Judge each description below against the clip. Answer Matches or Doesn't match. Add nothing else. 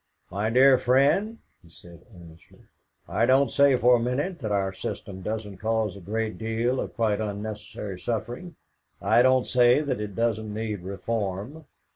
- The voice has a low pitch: Matches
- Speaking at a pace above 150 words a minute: Matches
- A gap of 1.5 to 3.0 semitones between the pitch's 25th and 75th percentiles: Doesn't match